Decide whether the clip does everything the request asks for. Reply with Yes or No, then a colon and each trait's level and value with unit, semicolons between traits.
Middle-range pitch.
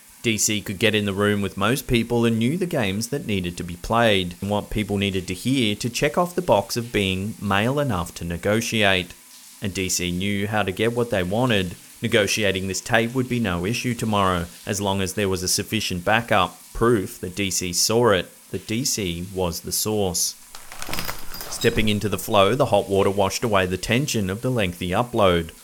No: low, 105 Hz